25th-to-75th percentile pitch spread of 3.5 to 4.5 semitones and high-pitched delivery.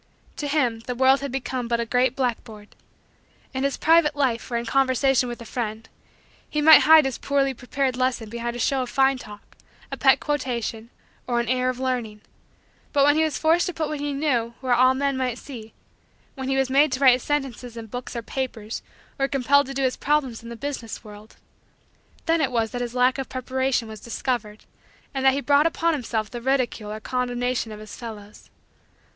No: average, 2.7 semitones; very high, 255 Hz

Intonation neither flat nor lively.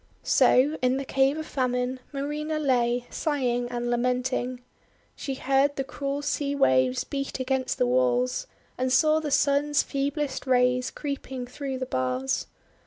No: narrow, 2.3 semitones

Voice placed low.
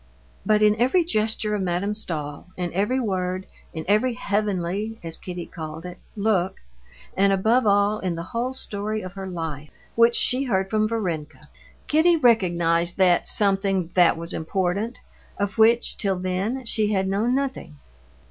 No: high, 200 Hz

